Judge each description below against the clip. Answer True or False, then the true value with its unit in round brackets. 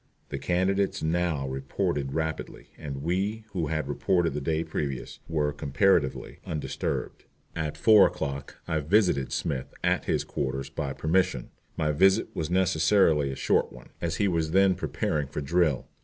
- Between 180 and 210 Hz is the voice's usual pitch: False (80 Hz)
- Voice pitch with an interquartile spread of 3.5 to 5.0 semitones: True (4.2 semitones)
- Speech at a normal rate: True (155 wpm)